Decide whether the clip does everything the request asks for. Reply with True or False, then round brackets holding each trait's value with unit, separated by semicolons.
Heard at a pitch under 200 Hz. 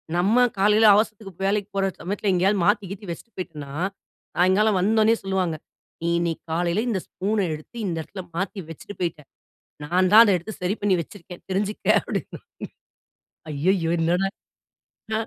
True (190 Hz)